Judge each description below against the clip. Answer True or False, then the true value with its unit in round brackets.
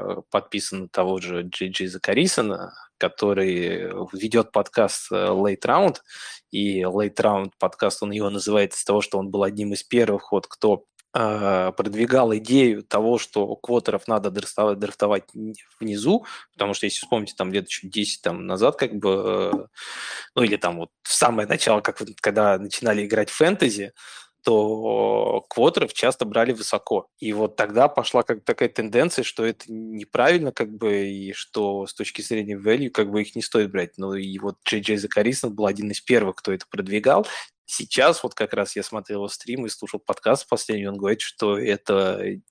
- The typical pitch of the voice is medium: False (105 Hz)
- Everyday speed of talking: False (175 wpm)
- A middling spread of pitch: False (1.6 semitones)